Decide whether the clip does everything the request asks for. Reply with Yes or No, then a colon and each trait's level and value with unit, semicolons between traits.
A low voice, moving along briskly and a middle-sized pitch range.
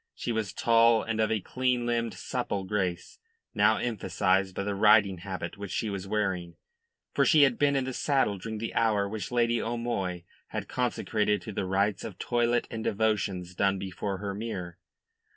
No: low, 105 Hz; average, 180 wpm; average, 3.3 semitones